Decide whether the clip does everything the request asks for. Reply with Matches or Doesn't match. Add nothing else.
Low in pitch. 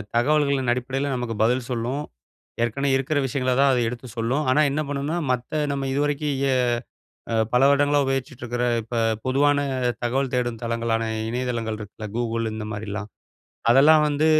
Matches